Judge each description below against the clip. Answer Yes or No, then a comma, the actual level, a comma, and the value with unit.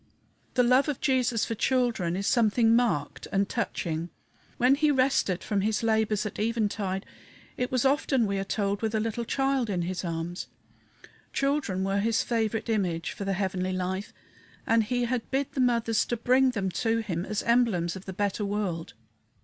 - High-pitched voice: Yes, high, 220 Hz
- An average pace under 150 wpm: No, average, 180 wpm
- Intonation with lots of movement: No, average, 4.1 semitones